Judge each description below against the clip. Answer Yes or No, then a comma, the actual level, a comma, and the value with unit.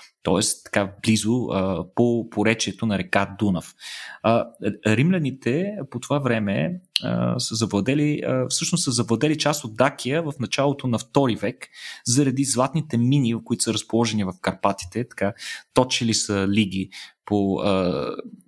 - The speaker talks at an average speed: Yes, average, 140 wpm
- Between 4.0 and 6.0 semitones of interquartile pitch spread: Yes, average, 4.9 semitones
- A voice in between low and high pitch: No, low, 115 Hz